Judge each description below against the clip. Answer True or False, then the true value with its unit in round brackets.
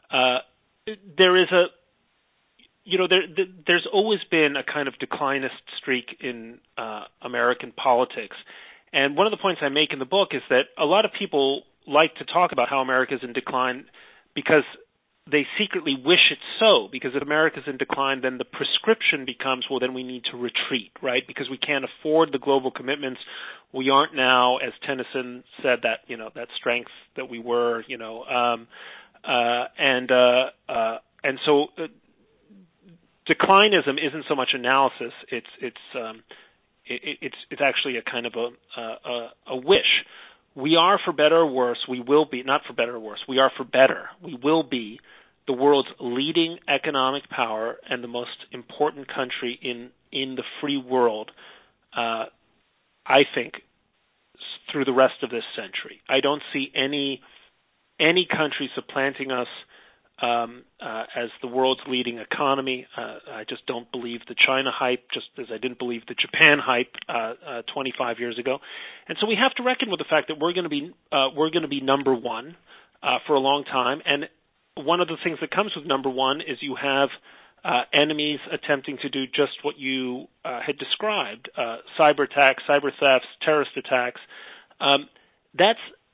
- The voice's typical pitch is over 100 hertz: True (135 Hz)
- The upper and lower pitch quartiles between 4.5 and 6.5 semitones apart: False (3.6 semitones)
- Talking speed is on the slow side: False (180 wpm)